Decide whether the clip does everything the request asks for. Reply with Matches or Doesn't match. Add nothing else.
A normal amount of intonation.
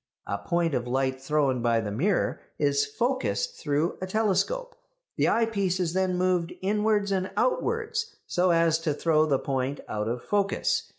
Doesn't match